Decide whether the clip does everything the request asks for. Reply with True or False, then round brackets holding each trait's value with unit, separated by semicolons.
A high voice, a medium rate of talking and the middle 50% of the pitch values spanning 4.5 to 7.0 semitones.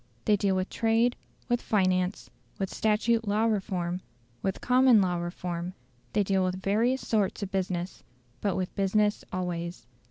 False (195 Hz; 150 wpm; 2.9 semitones)